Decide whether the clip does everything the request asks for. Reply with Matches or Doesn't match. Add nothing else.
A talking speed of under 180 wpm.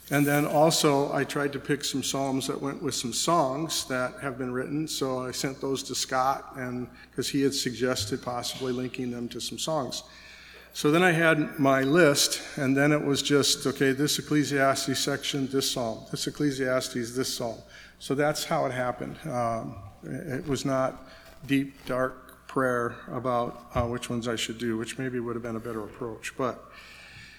Doesn't match